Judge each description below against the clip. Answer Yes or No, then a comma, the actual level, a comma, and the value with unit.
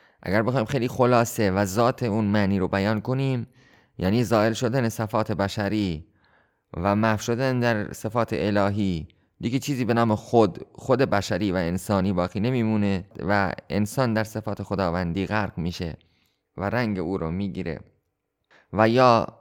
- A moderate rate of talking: Yes, average, 145 wpm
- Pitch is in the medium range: No, low, 105 Hz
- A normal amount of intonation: Yes, average, 3.2 semitones